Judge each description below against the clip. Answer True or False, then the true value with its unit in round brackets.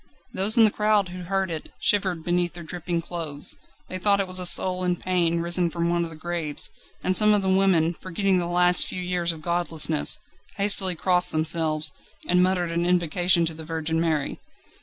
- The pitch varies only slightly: True (1.9 semitones)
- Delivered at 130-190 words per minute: False (200 wpm)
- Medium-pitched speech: True (175 Hz)